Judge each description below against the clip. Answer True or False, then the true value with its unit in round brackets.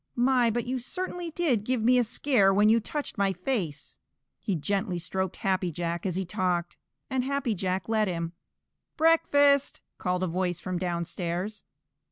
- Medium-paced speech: True (165 wpm)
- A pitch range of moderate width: False (5.7 semitones)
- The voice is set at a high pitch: True (200 Hz)